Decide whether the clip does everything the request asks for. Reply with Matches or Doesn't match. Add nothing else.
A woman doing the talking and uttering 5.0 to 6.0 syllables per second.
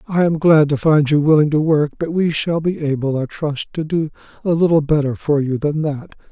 Doesn't match